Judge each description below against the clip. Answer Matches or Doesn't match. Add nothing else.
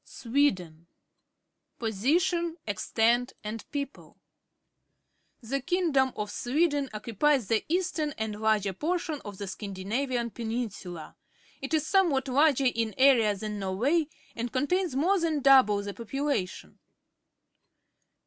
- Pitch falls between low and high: Doesn't match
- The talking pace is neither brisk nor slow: Doesn't match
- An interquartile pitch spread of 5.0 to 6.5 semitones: Matches